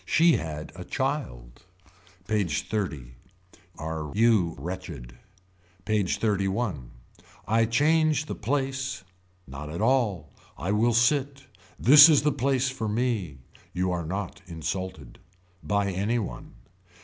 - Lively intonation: Yes, wide, 7.1 semitones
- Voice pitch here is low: Yes, low, 105 Hz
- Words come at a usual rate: No, slow, 120 wpm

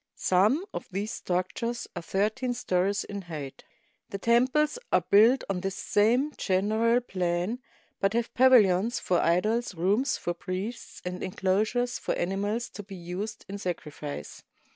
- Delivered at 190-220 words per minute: No, average, 145 wpm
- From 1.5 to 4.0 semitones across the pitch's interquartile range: No, average, 4.4 semitones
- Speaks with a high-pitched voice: Yes, high, 200 Hz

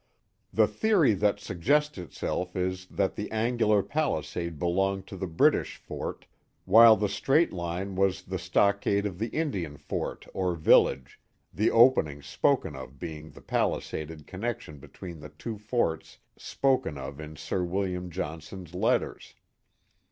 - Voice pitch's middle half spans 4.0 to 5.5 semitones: Yes, average, 4.4 semitones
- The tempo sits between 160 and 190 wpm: No, average, 140 wpm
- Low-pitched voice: Yes, very low, 95 Hz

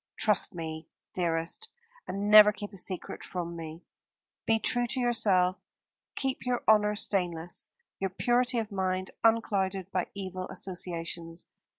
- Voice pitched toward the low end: No, high, 190 Hz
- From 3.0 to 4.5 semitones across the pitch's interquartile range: Yes, average, 3.6 semitones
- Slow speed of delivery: Yes, slow, 130 wpm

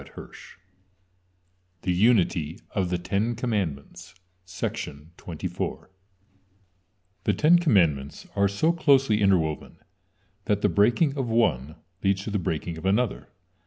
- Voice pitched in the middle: No, very low, 95 Hz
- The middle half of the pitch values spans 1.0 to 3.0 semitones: No, average, 3.8 semitones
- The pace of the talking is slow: Yes, slow, 105 wpm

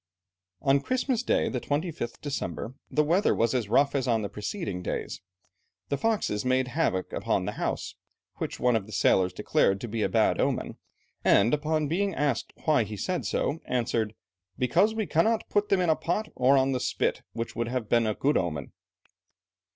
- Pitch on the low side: Yes, low, 130 Hz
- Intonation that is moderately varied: No, wide, 6.3 semitones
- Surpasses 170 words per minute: Yes, average, 190 wpm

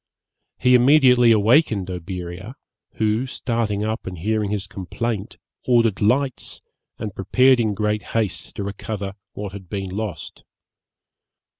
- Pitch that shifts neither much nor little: Yes, average, 3.3 semitones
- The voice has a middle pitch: No, low, 105 Hz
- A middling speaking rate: No, slow, 125 wpm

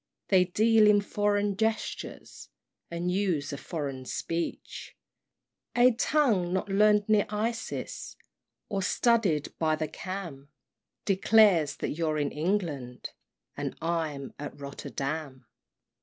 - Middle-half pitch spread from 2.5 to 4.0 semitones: No, wide, 5.4 semitones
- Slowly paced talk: Yes, slow, 110 wpm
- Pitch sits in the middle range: Yes, medium, 180 Hz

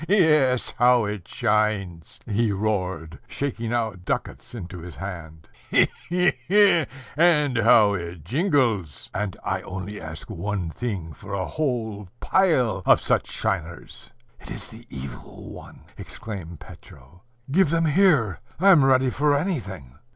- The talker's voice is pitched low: Yes, low, 110 Hz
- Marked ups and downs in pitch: Yes, wide, 7.5 semitones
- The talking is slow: No, average, 145 wpm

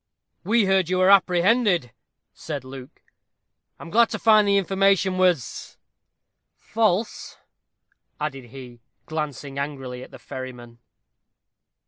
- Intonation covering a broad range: Yes, wide, 6.8 semitones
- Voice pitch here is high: No, medium, 170 Hz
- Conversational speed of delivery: No, slow, 115 wpm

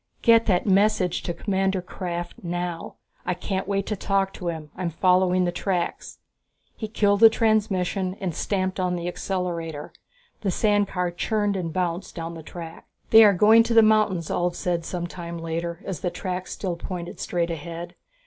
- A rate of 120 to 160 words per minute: No, average, 175 wpm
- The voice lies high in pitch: No, medium, 180 Hz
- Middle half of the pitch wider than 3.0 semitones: No, narrow, 2.5 semitones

